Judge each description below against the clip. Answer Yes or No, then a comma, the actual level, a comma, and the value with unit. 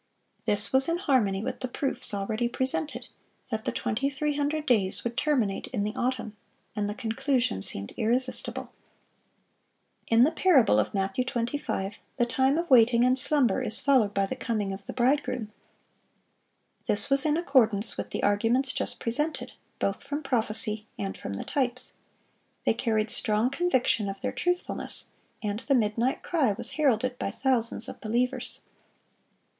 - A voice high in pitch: Yes, high, 240 Hz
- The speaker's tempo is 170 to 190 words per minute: No, average, 155 wpm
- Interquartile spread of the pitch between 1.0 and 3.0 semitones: No, average, 4.2 semitones